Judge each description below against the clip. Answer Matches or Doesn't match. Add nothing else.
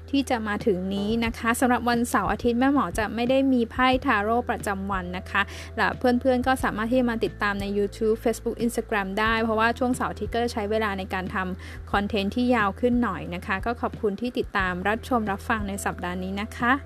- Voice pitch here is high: Matches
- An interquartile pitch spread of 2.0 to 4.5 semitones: Matches